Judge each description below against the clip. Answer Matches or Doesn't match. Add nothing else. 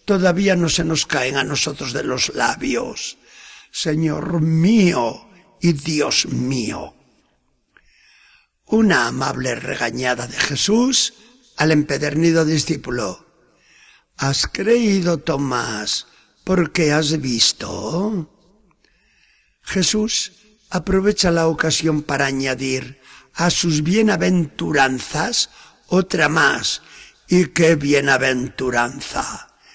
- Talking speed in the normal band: Doesn't match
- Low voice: Doesn't match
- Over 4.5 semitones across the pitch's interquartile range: Matches